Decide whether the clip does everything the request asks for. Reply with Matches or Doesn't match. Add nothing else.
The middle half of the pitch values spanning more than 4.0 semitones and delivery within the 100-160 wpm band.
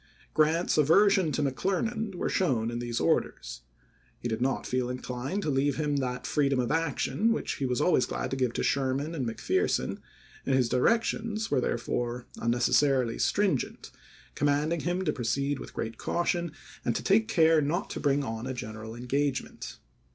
Doesn't match